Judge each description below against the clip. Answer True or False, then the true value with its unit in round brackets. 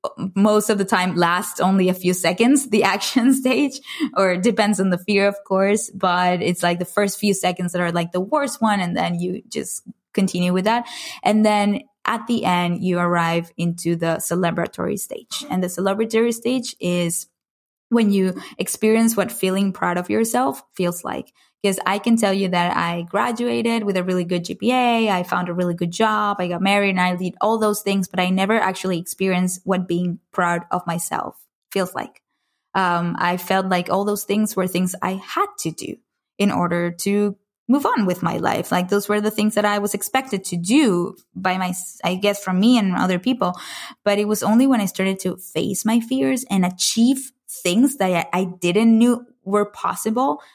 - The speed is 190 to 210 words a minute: True (200 wpm)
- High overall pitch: True (195 Hz)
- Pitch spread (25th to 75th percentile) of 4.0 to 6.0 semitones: False (3.5 semitones)